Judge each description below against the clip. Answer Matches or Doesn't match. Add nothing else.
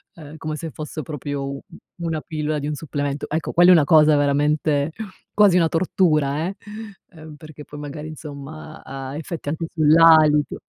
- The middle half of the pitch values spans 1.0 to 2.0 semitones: Matches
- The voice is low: Doesn't match